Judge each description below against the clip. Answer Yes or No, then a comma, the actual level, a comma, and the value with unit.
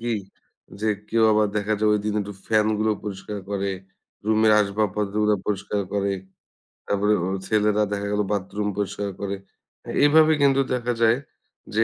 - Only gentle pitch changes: Yes, narrow, 1.3 semitones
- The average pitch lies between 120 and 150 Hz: No, low, 105 Hz